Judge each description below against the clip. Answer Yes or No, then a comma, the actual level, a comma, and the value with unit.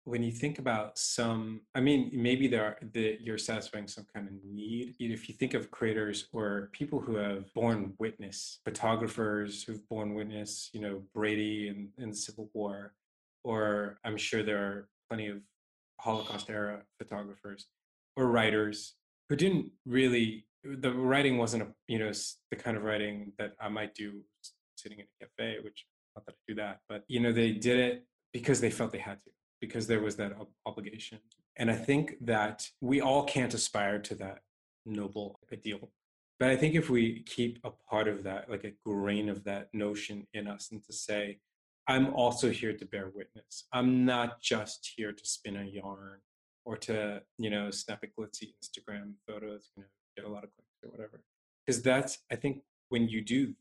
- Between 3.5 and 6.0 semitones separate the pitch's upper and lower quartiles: No, narrow, 2.4 semitones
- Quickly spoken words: No, average, 195 wpm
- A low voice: Yes, low, 110 Hz